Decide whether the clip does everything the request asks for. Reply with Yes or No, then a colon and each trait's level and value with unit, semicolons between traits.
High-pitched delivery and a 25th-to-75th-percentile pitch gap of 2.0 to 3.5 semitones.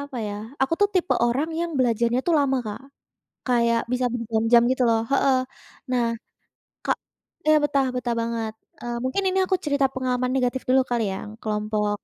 Yes: very high, 250 Hz; average, 2.9 semitones